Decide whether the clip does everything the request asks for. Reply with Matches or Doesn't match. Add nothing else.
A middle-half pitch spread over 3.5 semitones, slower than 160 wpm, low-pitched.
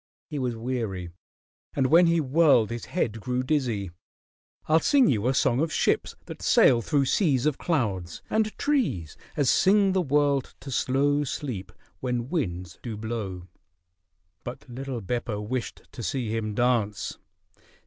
Matches